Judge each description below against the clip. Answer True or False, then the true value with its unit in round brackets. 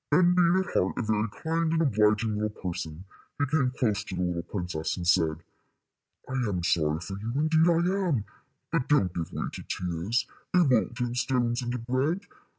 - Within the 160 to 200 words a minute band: True (185 wpm)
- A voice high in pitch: False (120 Hz)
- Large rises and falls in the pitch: True (8.6 semitones)